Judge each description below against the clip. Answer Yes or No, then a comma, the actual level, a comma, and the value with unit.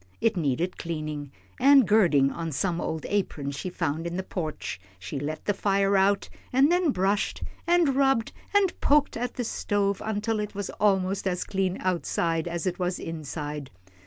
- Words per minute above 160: Yes, average, 175 wpm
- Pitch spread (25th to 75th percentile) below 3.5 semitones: No, average, 4.7 semitones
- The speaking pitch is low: No, high, 190 Hz